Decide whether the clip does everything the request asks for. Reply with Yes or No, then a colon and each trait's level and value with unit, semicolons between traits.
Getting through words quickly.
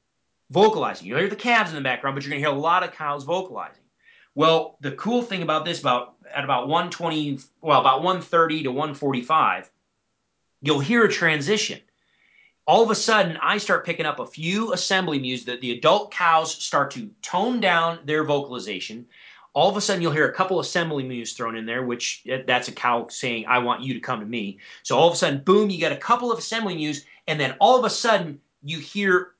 Yes: fast, 220 wpm